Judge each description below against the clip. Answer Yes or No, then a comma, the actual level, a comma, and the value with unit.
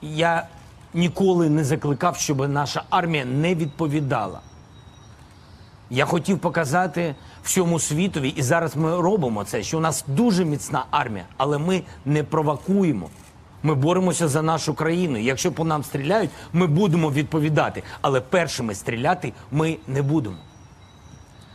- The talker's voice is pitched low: No, medium, 155 Hz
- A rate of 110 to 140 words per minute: Yes, average, 130 wpm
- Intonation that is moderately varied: Yes, average, 3.8 semitones